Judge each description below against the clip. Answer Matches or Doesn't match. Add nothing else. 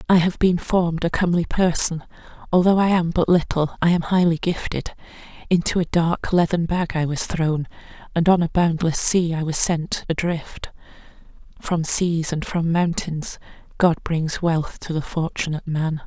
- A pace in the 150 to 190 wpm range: Matches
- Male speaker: Doesn't match